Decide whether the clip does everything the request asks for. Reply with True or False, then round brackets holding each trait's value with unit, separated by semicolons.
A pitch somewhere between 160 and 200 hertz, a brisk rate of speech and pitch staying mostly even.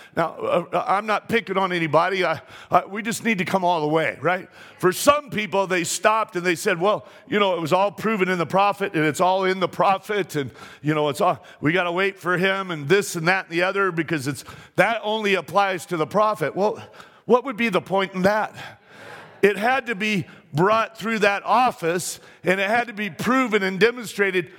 False (190 Hz; 220 wpm; 3.3 semitones)